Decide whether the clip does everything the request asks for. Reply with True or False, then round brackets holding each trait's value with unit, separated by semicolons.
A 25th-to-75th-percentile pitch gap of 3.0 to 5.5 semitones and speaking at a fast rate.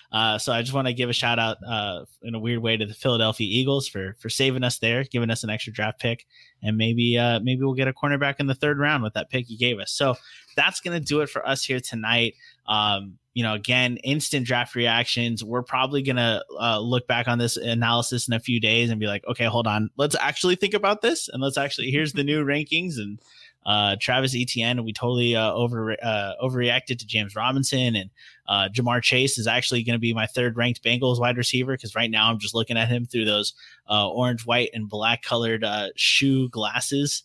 False (2.6 semitones; 230 wpm)